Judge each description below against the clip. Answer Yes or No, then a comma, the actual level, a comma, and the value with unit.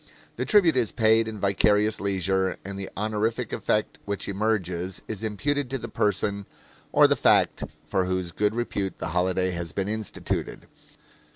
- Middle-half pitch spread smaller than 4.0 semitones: Yes, average, 2.7 semitones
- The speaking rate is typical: Yes, average, 160 wpm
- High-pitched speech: No, low, 100 Hz